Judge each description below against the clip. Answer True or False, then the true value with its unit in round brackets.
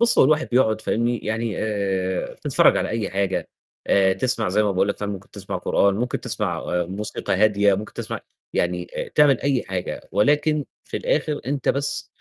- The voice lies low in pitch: True (105 Hz)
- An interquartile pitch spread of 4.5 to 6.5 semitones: True (4.9 semitones)